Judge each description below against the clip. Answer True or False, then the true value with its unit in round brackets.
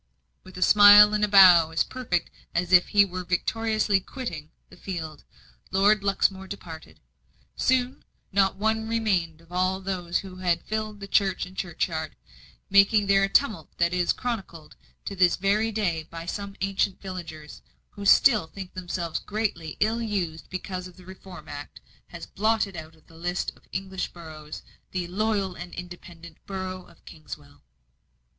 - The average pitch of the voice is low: False (185 Hz)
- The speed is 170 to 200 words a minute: False (155 wpm)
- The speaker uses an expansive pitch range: False (3.0 semitones)